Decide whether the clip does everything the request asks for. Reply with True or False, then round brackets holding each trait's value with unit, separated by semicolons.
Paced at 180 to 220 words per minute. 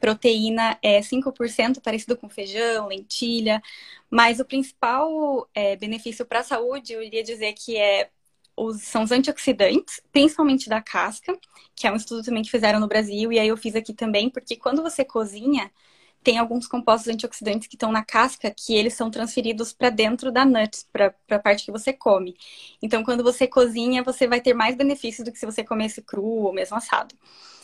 True (185 wpm)